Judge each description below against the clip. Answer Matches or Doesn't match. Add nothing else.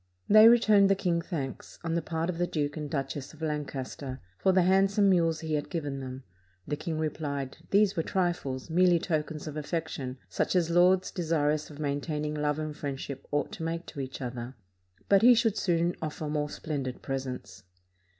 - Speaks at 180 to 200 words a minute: Matches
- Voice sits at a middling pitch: Matches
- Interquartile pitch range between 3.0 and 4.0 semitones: Matches